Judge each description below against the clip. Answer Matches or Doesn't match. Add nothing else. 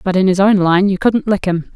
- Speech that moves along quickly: Matches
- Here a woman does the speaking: Matches